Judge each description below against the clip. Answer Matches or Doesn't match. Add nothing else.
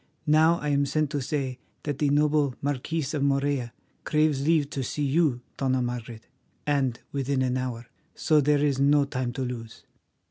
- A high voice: Doesn't match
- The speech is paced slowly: Doesn't match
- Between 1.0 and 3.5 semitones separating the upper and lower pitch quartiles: Matches